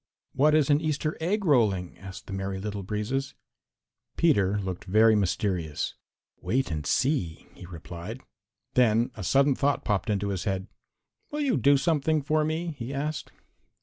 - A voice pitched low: Yes, low, 115 Hz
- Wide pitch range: Yes, wide, 7.3 semitones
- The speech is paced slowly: No, average, 155 wpm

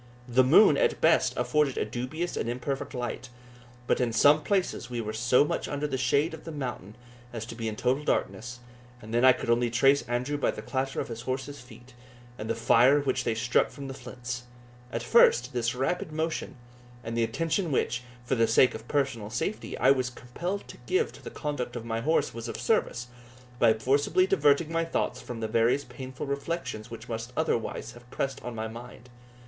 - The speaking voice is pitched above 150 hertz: No, low, 125 Hz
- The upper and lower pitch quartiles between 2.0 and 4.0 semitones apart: Yes, average, 3.5 semitones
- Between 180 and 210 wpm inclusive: Yes, fast, 205 wpm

